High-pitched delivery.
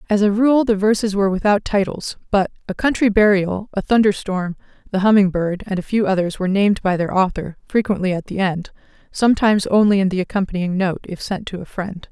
Yes: high, 200 Hz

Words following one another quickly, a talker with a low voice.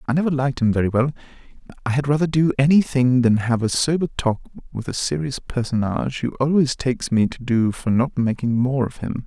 Yes: fast, 215 wpm; low, 130 Hz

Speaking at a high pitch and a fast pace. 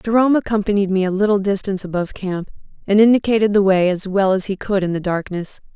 Yes: high, 195 Hz; fast, 210 wpm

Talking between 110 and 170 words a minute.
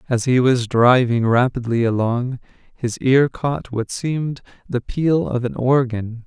Yes: average, 155 wpm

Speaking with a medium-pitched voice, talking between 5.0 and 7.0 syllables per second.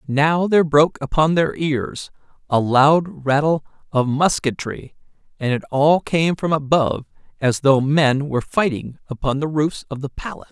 No: medium, 150 Hz; 4.7 syllables/s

